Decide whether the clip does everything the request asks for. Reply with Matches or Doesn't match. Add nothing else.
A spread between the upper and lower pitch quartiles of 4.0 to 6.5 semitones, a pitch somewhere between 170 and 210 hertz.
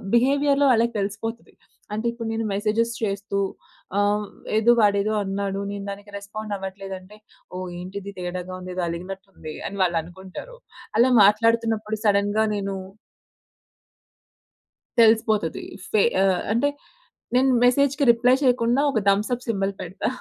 Doesn't match